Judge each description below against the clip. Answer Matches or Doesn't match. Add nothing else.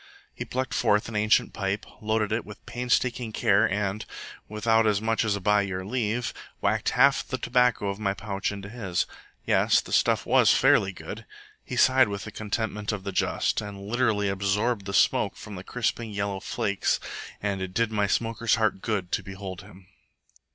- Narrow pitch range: Matches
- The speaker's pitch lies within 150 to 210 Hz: Doesn't match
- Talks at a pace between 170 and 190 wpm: Matches